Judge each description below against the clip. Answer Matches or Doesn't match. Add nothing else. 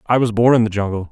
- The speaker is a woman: Doesn't match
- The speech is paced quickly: Matches